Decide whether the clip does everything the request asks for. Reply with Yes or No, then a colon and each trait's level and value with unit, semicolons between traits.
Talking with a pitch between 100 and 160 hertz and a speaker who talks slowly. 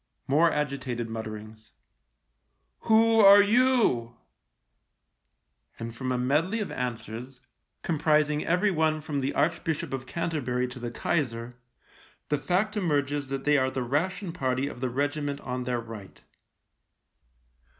No: medium, 140 Hz; average, 145 wpm